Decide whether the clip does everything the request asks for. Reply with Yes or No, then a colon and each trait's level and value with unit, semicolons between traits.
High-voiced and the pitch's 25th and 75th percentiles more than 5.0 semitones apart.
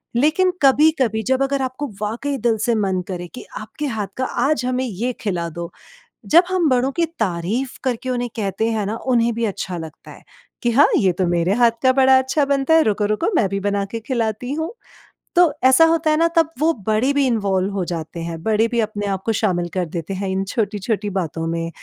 Yes: high, 230 Hz; wide, 5.5 semitones